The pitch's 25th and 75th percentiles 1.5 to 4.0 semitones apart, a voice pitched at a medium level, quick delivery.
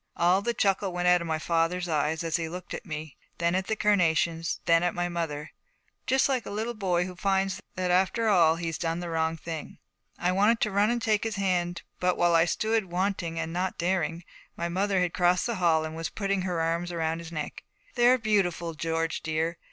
Yes: average, 2.8 semitones; medium, 175 Hz; fast, 215 wpm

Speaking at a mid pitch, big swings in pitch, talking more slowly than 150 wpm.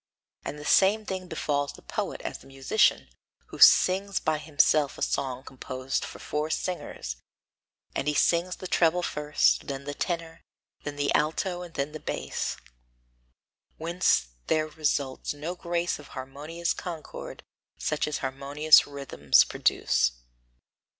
No: medium, 150 Hz; average, 3.4 semitones; average, 140 wpm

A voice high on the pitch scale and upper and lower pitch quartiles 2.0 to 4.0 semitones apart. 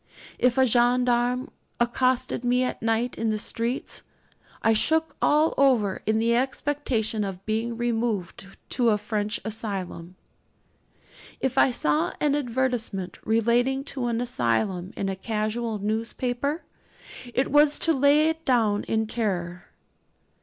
Yes: high, 235 Hz; average, 3.3 semitones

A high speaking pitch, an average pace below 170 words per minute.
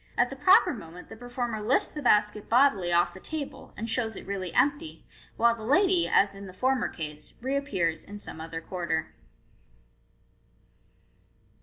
Yes: high, 215 Hz; average, 160 wpm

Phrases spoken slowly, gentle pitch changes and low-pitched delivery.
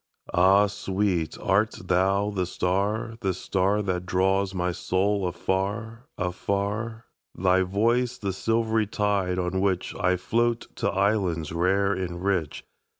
Yes: slow, 115 wpm; narrow, 2.3 semitones; very low, 95 Hz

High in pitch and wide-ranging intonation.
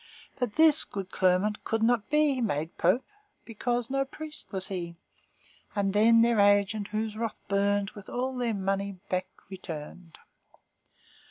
No: high, 210 Hz; average, 3.7 semitones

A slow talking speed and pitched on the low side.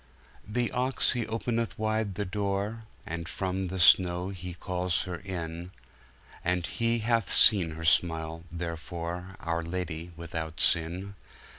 Yes: slow, 120 wpm; very low, 90 Hz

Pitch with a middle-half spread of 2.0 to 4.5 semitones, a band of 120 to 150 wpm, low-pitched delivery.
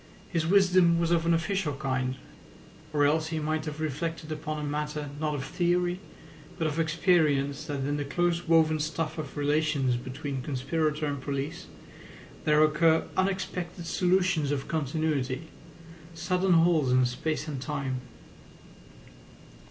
No: average, 2.7 semitones; average, 140 wpm; medium, 155 Hz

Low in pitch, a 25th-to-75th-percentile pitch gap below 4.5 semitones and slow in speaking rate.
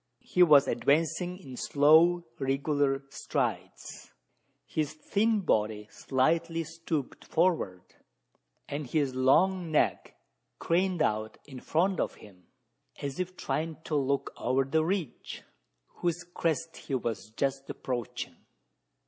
No: medium, 150 Hz; average, 4.1 semitones; slow, 115 wpm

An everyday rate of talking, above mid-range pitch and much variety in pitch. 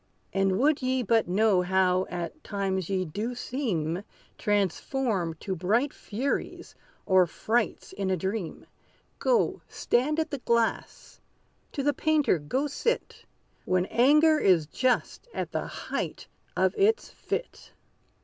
No: slow, 130 wpm; high, 215 Hz; wide, 6.5 semitones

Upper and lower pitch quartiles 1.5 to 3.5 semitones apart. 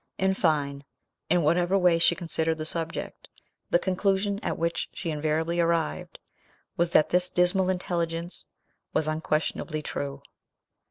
Yes: narrow, 2.4 semitones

